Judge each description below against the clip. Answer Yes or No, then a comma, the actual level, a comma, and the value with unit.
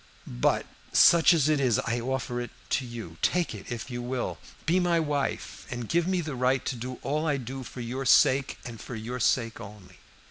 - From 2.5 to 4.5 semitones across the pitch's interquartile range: Yes, average, 3.7 semitones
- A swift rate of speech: Yes, fast, 210 wpm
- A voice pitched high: No, low, 130 Hz